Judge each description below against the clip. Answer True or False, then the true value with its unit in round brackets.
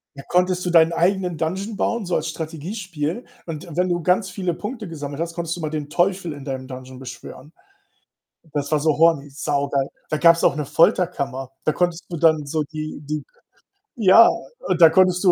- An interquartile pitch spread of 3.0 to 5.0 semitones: True (3.5 semitones)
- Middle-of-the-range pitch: True (165 Hz)